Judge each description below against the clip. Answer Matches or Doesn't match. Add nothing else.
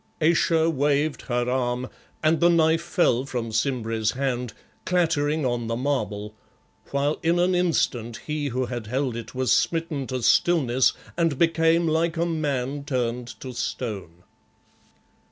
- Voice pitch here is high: Doesn't match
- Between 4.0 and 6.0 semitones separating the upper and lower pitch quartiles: Matches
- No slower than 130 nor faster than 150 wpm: Matches